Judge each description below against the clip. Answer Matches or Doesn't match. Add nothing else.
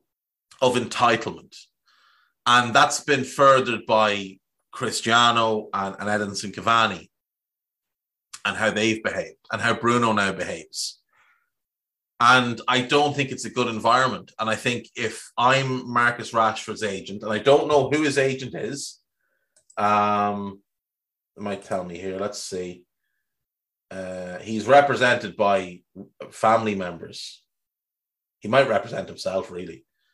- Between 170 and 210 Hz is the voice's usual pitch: Doesn't match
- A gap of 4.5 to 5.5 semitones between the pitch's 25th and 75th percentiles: Doesn't match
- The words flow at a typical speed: Doesn't match